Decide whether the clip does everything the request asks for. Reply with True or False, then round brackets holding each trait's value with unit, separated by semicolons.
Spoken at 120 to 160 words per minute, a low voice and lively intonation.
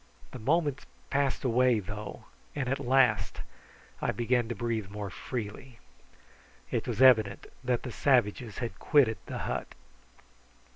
False (135 wpm; 120 Hz; 3.2 semitones)